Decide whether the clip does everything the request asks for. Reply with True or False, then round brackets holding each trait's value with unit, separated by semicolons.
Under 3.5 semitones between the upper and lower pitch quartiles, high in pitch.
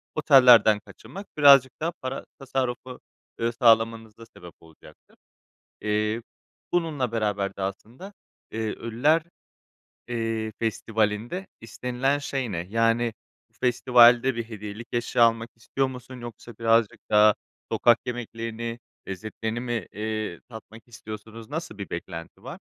False (2.5 semitones; 115 Hz)